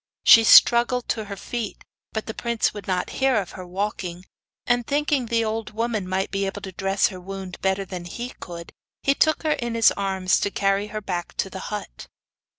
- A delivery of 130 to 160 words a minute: No, fast, 205 wpm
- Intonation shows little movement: No, average, 3.6 semitones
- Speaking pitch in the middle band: No, high, 205 Hz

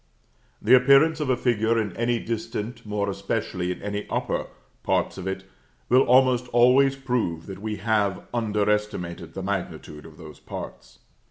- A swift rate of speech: No, average, 160 wpm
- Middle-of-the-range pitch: No, low, 110 Hz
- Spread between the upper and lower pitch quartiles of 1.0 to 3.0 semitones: No, average, 4.2 semitones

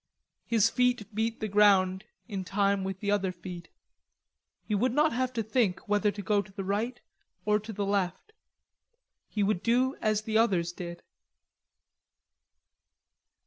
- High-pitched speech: Yes, high, 205 Hz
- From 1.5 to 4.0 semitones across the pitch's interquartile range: Yes, average, 2.7 semitones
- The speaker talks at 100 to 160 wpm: Yes, average, 150 wpm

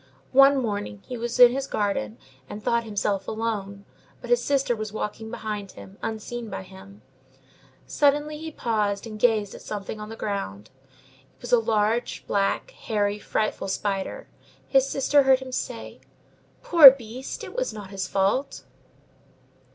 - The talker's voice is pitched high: Yes, high, 220 Hz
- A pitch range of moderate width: Yes, average, 4.2 semitones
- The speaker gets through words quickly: No, average, 155 wpm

